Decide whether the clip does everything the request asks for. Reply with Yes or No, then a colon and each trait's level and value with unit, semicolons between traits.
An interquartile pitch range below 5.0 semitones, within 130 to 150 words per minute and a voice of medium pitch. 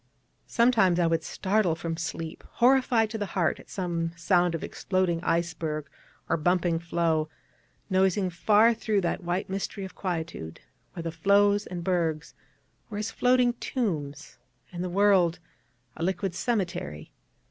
Yes: average, 3.4 semitones; average, 145 wpm; medium, 180 Hz